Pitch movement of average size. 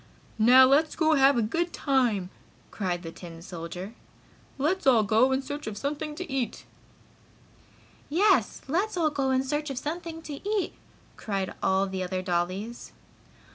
No: wide, 7.5 semitones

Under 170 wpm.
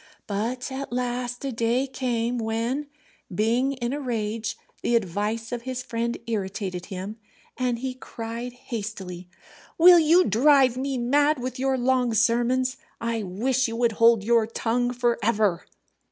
Yes: average, 150 wpm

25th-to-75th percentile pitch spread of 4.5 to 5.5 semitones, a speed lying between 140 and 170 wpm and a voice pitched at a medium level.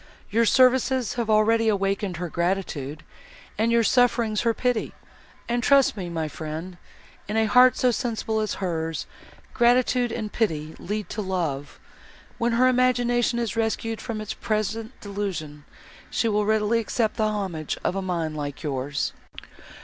No: average, 4.9 semitones; average, 150 wpm; high, 215 Hz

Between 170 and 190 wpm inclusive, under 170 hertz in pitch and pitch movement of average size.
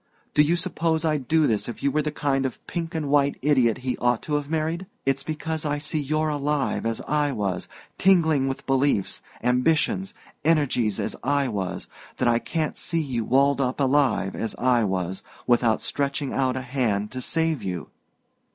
Yes: average, 185 wpm; medium, 140 Hz; average, 3.8 semitones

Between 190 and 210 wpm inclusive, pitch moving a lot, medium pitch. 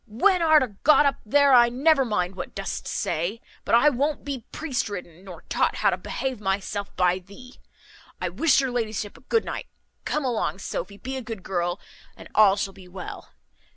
No: average, 195 wpm; wide, 6.0 semitones; high, 225 Hz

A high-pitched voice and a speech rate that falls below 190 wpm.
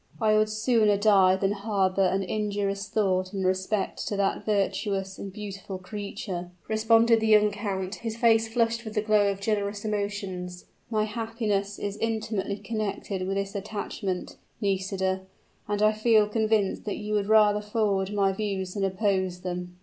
Yes: high, 205 Hz; average, 160 wpm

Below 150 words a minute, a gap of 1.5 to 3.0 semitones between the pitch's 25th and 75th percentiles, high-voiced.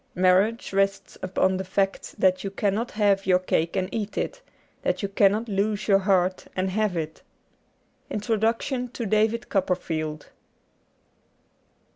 Yes: average, 140 wpm; narrow, 2.5 semitones; high, 195 Hz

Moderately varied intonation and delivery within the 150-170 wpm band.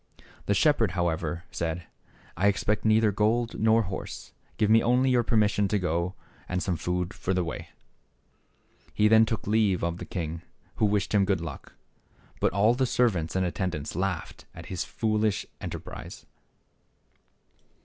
Yes: average, 3.8 semitones; average, 165 wpm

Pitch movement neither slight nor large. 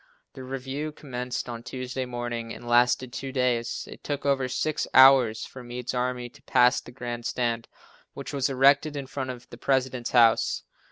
No: narrow, 1.8 semitones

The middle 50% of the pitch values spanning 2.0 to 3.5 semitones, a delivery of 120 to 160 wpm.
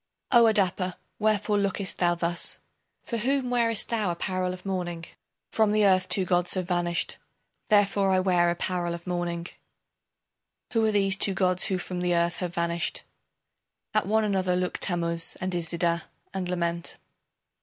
Yes: average, 2.7 semitones; average, 155 wpm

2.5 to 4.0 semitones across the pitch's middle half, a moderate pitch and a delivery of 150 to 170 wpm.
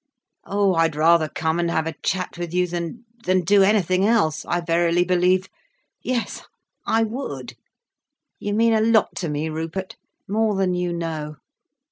Yes: average, 3.7 semitones; medium, 180 Hz; average, 155 wpm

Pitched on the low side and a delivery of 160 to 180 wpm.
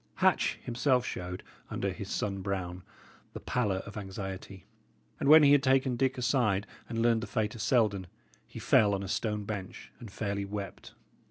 Yes: low, 105 Hz; average, 175 wpm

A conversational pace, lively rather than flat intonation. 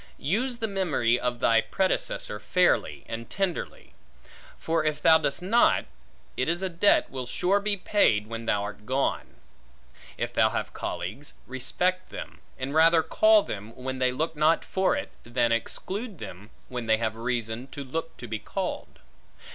Yes: average, 165 wpm; wide, 7.7 semitones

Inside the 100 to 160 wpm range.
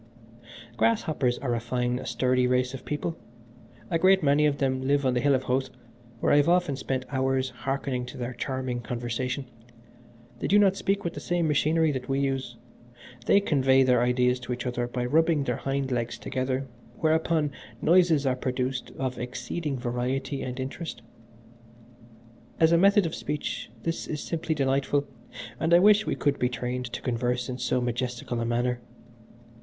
No: average, 175 wpm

